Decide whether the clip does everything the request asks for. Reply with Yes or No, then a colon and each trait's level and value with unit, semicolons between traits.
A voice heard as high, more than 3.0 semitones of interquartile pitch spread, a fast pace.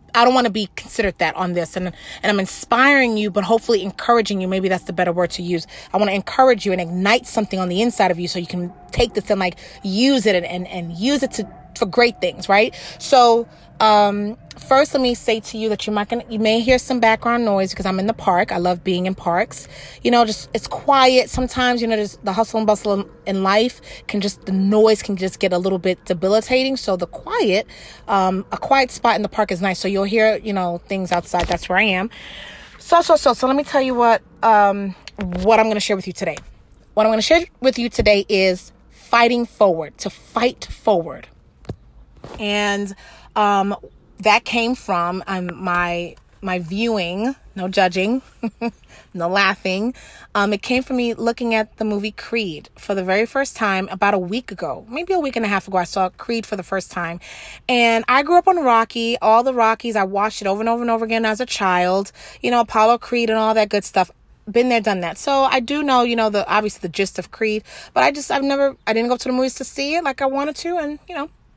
Yes: high, 215 Hz; average, 3.9 semitones; fast, 230 wpm